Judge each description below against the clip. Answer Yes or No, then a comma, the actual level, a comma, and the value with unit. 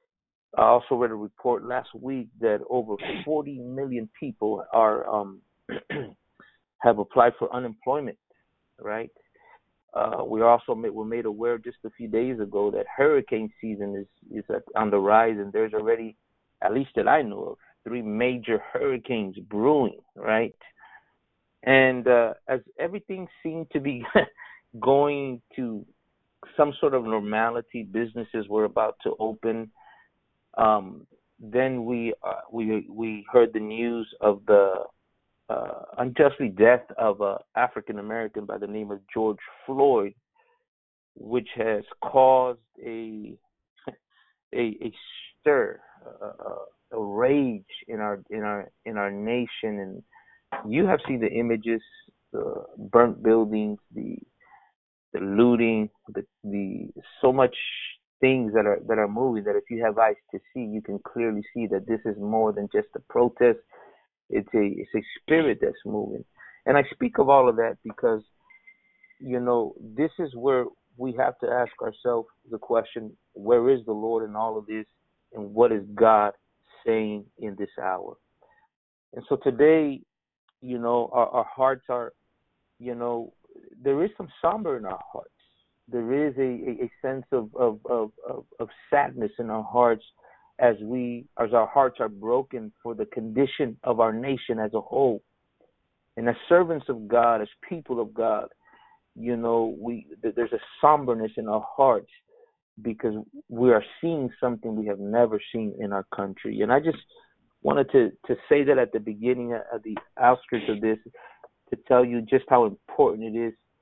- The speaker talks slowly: No, average, 155 wpm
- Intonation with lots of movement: No, average, 3.4 semitones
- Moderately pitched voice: No, low, 120 Hz